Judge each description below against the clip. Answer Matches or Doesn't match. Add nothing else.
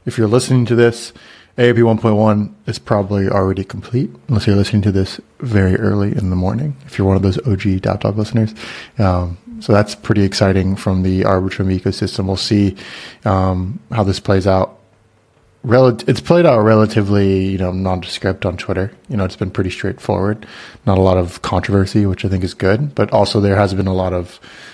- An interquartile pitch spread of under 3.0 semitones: Matches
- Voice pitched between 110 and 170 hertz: Doesn't match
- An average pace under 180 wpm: Doesn't match